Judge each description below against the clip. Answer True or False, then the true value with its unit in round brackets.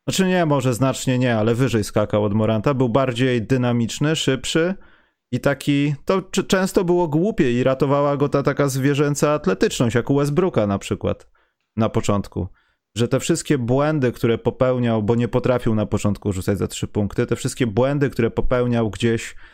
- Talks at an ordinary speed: False (170 wpm)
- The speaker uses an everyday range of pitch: True (4.2 semitones)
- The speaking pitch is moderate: False (130 Hz)